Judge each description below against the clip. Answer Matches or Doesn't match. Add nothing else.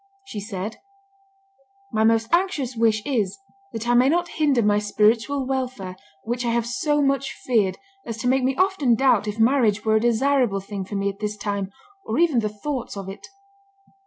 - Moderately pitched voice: Doesn't match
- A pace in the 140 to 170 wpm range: Doesn't match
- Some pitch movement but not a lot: Matches